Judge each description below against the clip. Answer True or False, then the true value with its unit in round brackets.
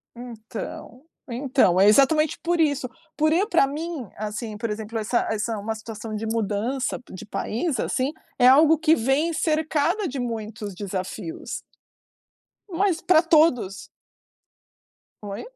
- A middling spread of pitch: False (6.4 semitones)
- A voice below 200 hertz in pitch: False (245 Hz)